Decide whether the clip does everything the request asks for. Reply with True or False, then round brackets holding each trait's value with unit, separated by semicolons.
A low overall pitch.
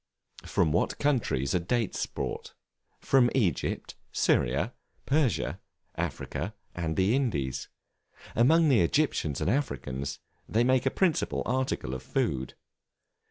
True (110 Hz)